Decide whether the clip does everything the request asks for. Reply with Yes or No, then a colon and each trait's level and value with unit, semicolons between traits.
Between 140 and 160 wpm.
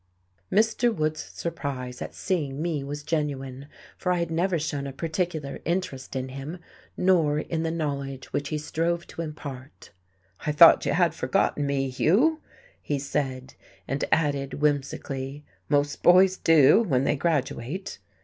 Yes: average, 150 wpm